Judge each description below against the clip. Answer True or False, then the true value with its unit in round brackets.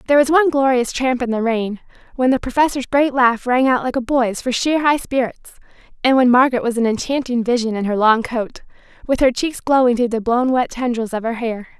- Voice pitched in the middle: False (250 Hz)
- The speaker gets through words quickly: True (230 wpm)